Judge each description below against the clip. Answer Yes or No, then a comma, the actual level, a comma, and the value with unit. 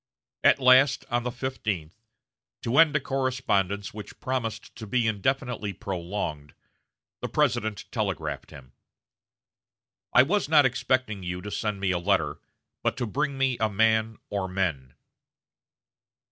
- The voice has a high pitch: No, low, 110 Hz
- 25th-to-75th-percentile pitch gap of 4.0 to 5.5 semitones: Yes, average, 5.0 semitones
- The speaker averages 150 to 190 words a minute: No, slow, 135 wpm